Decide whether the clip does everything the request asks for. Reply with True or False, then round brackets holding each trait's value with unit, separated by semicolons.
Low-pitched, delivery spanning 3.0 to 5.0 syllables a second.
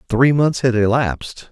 True (125 Hz; 4.5 syllables/s)